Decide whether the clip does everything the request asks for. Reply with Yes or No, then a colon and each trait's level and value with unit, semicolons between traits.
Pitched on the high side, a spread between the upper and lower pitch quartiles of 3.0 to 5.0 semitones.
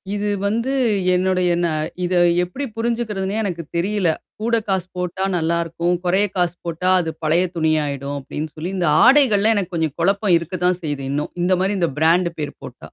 No: medium, 180 Hz; average, 3.3 semitones